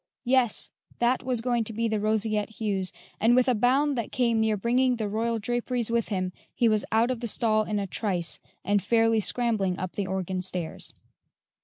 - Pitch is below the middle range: No, high, 220 Hz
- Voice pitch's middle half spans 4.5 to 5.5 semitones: No, average, 2.7 semitones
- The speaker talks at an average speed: Yes, average, 195 wpm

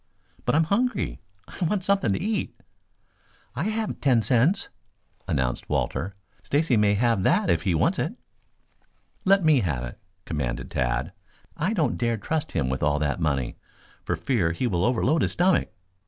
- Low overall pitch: Yes, low, 115 Hz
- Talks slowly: No, average, 165 wpm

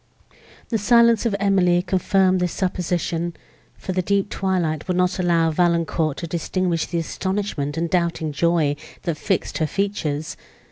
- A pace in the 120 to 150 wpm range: Yes, average, 145 wpm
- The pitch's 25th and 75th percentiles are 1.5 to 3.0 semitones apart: Yes, narrow, 2.5 semitones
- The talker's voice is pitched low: No, medium, 175 Hz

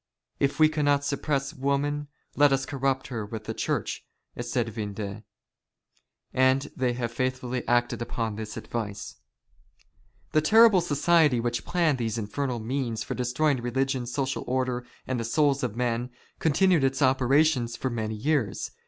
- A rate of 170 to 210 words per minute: No, average, 145 wpm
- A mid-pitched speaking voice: No, low, 130 Hz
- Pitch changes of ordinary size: Yes, average, 3.3 semitones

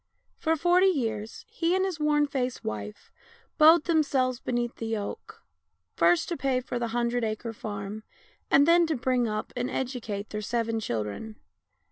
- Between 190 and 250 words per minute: No, average, 165 wpm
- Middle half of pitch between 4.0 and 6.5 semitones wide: Yes, wide, 5.6 semitones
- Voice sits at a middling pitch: No, high, 245 Hz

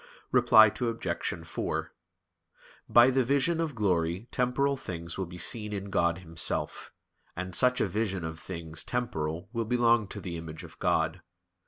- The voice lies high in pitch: No, very low, 95 Hz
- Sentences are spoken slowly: No, average, 155 wpm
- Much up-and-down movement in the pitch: Yes, wide, 6.1 semitones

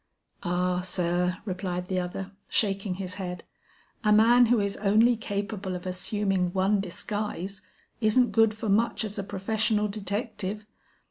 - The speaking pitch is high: Yes, high, 200 Hz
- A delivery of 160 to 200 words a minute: No, average, 140 wpm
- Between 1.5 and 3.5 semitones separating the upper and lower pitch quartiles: Yes, average, 2.7 semitones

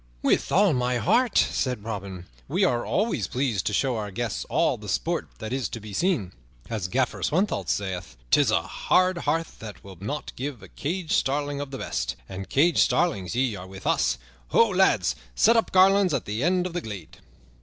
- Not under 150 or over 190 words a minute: No, average, 200 wpm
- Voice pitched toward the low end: Yes, low, 125 Hz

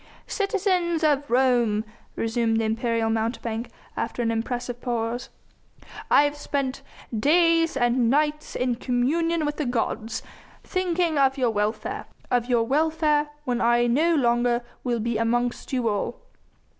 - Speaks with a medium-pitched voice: No, high, 245 Hz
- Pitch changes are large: No, average, 4.4 semitones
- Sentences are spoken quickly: No, slow, 135 wpm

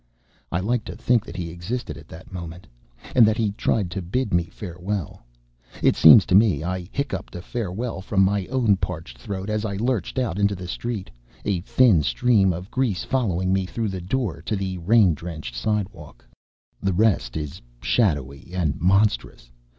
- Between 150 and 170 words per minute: No, average, 180 wpm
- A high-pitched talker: No, very low, 95 Hz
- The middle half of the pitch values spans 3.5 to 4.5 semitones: Yes, average, 4.0 semitones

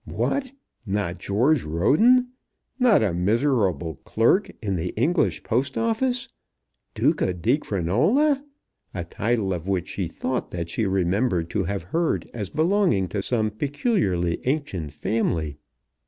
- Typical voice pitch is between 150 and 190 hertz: No, low, 110 Hz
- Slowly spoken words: Yes, slow, 130 wpm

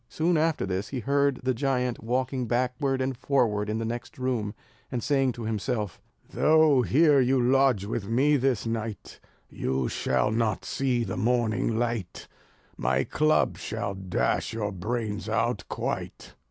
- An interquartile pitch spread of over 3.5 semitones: Yes, average, 3.9 semitones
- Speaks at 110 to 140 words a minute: No, average, 155 wpm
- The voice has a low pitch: Yes, low, 120 Hz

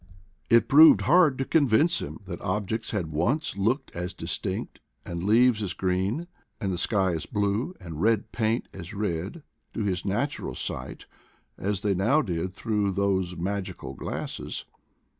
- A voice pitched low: Yes, low, 100 Hz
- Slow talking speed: No, average, 155 wpm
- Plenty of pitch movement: No, average, 4.0 semitones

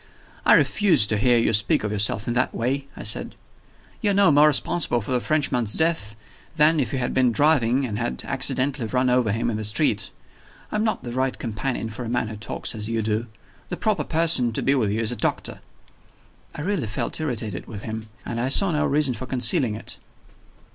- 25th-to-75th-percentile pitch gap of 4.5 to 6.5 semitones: Yes, average, 4.9 semitones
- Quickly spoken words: Yes, fast, 215 wpm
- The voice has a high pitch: No, low, 125 Hz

